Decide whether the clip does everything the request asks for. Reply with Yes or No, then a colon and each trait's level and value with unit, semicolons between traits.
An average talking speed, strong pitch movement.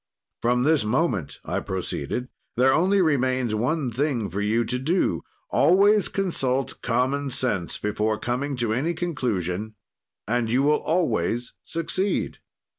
No: slow, 130 wpm; wide, 5.9 semitones